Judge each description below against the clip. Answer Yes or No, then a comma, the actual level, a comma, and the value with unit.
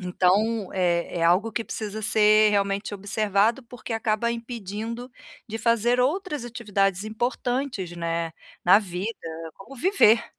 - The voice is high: Yes, high, 215 Hz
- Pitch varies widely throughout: No, average, 3.1 semitones